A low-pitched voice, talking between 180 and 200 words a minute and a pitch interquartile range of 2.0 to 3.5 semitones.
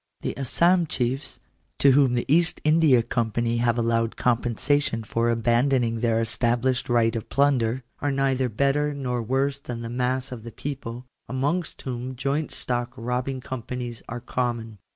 No: low, 125 Hz; average, 150 wpm; average, 2.7 semitones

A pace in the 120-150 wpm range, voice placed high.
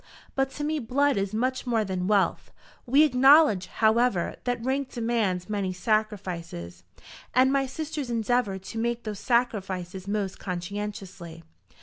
Yes: slow, 135 wpm; high, 220 Hz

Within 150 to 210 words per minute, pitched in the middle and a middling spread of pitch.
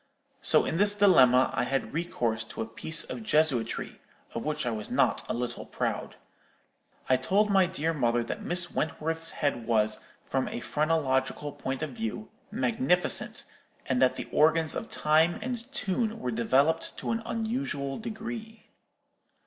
No: average, 155 wpm; medium, 155 Hz; wide, 8.1 semitones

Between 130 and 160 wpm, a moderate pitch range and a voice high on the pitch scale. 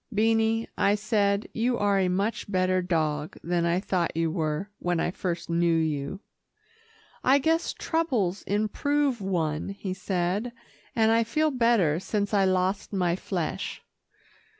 Yes: average, 145 wpm; average, 4.3 semitones; high, 195 Hz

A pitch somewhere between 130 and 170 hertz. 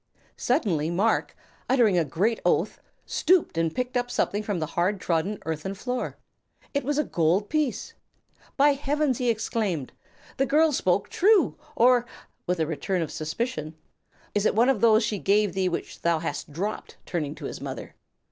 No: high, 205 Hz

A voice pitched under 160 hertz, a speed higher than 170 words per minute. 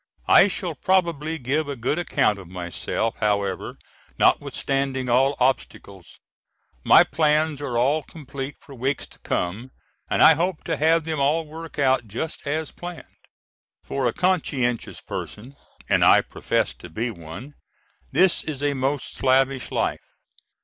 No: medium, 140 Hz; average, 145 wpm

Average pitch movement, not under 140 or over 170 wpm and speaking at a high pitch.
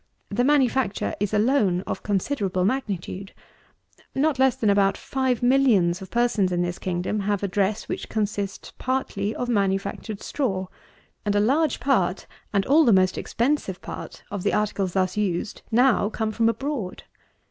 Yes: average, 4.6 semitones; average, 160 wpm; high, 210 Hz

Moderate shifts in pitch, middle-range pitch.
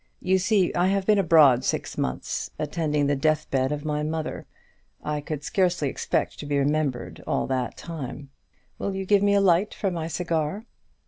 Yes: average, 4.3 semitones; medium, 155 Hz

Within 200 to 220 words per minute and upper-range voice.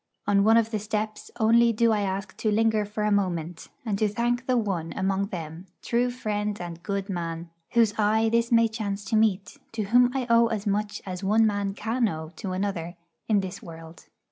Yes: fast, 205 wpm; high, 210 Hz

